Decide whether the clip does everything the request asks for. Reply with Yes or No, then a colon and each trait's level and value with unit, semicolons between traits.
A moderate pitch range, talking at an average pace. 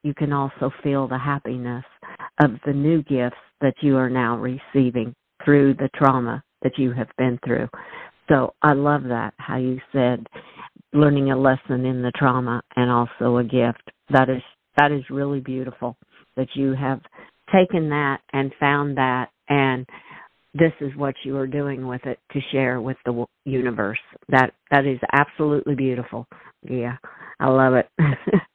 No: narrow, 2.1 semitones; average, 160 wpm